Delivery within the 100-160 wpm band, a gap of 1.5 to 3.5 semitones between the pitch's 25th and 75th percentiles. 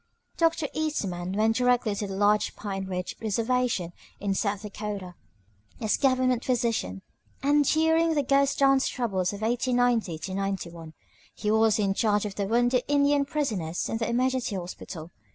No: average, 150 wpm; average, 4.8 semitones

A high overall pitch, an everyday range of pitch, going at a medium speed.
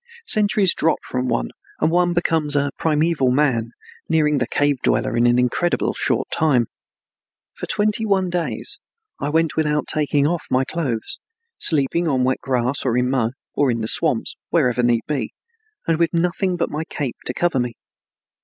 No: medium, 145 Hz; average, 4.9 semitones; average, 170 wpm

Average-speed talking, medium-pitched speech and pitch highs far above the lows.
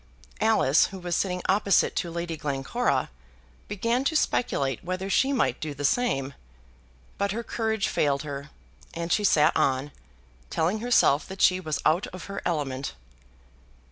Yes: average, 150 wpm; medium, 175 Hz; wide, 6.1 semitones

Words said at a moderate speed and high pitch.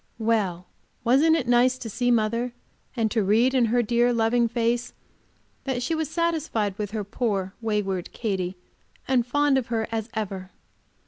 Yes: average, 165 wpm; high, 230 Hz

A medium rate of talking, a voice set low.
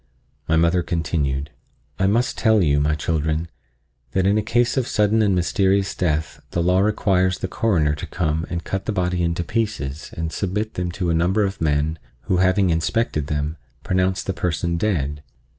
Yes: average, 180 wpm; very low, 90 Hz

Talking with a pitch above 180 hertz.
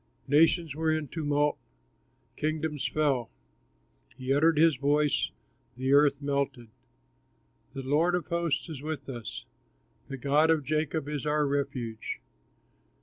No: medium, 145 Hz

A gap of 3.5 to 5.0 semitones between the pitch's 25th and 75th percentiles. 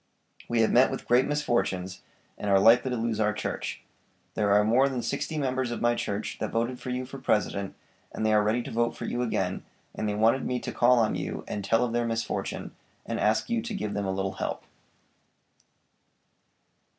No: average, 3.0 semitones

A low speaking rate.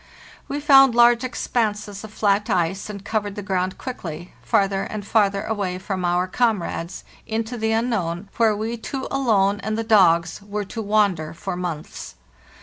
No: average, 165 wpm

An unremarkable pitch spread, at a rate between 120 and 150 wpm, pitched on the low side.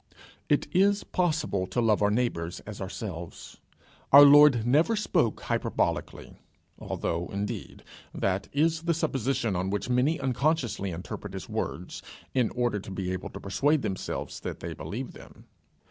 No: wide, 7.2 semitones; average, 145 wpm; low, 120 Hz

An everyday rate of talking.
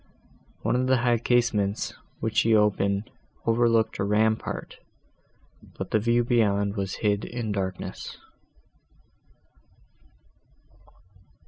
No: slow, 100 wpm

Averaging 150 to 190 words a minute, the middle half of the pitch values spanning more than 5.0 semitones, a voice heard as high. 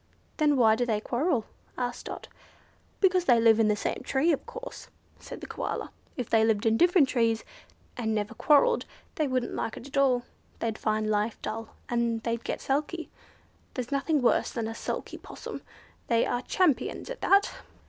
No: average, 180 wpm; average, 4.6 semitones; high, 245 Hz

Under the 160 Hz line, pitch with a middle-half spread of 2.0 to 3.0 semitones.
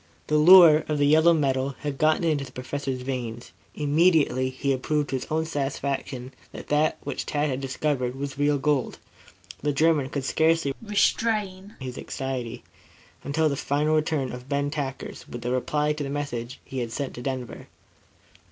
Yes: medium, 140 Hz; average, 2.7 semitones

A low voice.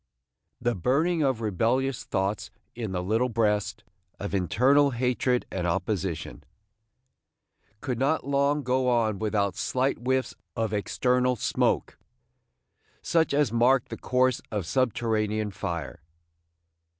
Yes: low, 120 Hz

